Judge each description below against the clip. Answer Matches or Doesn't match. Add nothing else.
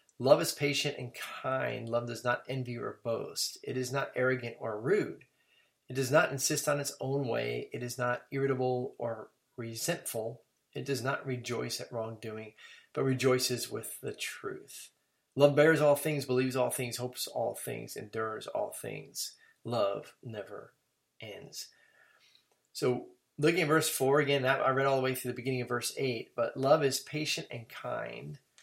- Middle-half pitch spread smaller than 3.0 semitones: Matches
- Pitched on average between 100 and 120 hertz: Doesn't match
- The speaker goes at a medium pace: Matches